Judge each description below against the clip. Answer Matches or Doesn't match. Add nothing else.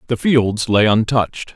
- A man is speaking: Matches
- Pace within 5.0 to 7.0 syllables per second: Doesn't match